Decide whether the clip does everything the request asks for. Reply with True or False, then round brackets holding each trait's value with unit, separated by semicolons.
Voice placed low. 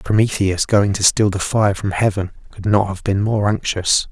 True (100 Hz)